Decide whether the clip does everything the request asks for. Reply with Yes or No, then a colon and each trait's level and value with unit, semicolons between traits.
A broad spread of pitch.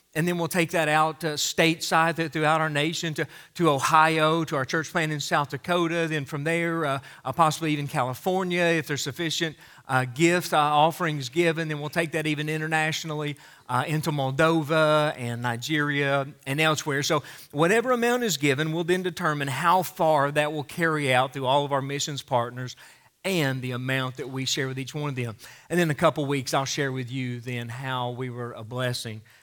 No: average, 3.2 semitones